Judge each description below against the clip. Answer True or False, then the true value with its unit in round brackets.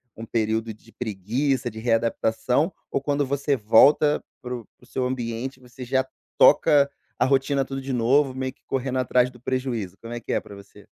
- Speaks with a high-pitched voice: False (125 Hz)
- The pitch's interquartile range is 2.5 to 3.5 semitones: True (2.9 semitones)